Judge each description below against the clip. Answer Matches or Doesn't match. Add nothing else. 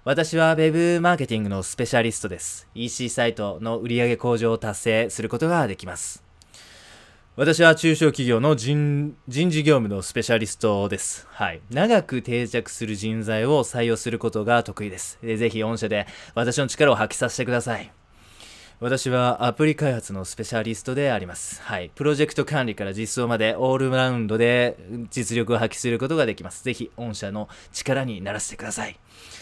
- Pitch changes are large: Doesn't match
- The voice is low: Matches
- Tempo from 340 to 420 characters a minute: Matches